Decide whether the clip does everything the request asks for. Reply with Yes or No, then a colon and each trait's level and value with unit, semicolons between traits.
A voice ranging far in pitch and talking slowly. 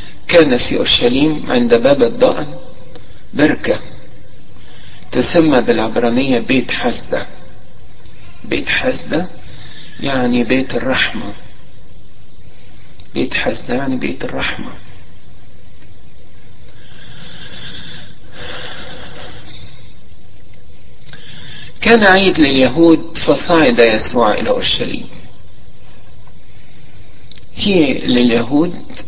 Yes: wide, 7.6 semitones; slow, 60 wpm